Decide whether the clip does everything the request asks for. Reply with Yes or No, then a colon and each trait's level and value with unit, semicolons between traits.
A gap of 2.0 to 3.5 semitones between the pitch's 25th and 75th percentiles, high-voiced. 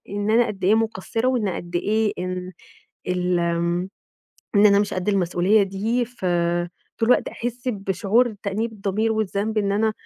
Yes: average, 3.1 semitones; high, 205 Hz